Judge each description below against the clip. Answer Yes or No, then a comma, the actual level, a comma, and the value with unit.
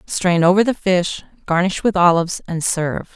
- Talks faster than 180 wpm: No, average, 170 wpm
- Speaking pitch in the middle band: Yes, medium, 180 Hz